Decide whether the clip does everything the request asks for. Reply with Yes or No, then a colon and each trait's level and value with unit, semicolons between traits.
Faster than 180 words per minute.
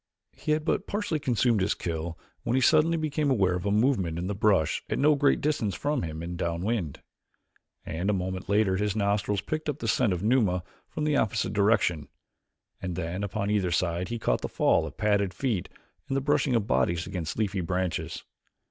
Yes: average, 200 wpm